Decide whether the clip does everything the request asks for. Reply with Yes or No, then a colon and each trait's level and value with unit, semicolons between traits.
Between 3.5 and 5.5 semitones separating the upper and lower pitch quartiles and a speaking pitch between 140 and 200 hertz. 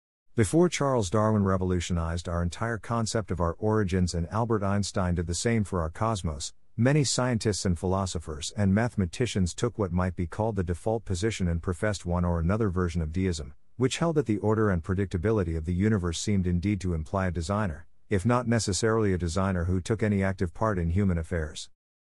No: average, 3.9 semitones; very low, 95 Hz